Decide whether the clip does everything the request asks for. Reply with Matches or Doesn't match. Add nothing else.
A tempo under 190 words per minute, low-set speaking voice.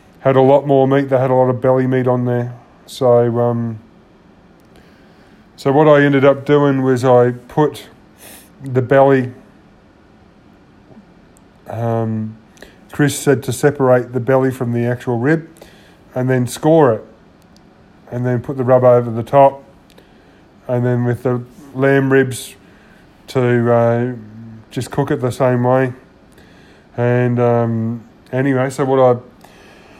Matches